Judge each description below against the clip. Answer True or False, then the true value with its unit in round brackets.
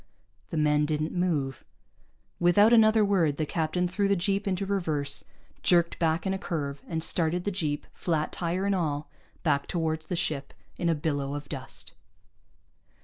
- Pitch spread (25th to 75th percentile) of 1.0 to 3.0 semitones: False (3.7 semitones)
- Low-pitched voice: False (165 Hz)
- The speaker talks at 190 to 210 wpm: False (165 wpm)